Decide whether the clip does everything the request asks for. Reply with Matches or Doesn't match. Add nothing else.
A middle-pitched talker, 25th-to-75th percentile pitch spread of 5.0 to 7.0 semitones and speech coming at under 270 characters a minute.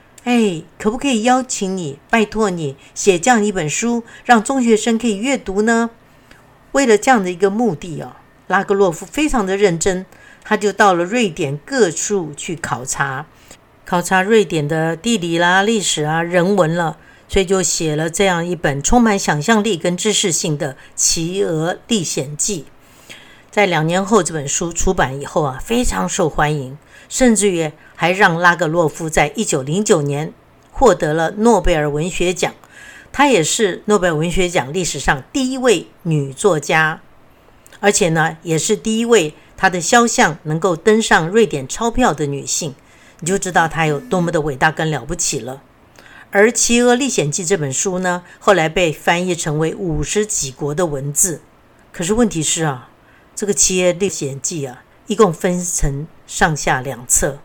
Matches